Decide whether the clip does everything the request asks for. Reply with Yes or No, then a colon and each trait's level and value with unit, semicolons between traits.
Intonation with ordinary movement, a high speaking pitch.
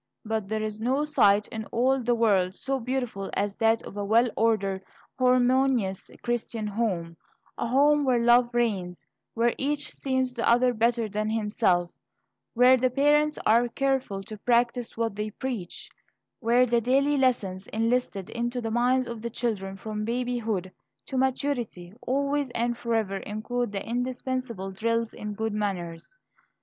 Yes: average, 3.1 semitones; high, 235 Hz